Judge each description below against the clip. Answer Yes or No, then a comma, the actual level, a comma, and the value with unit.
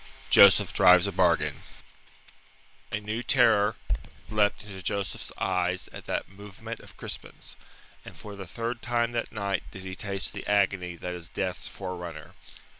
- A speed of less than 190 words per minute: Yes, average, 150 wpm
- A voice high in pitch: No, low, 100 Hz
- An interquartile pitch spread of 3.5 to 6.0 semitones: No, narrow, 2.6 semitones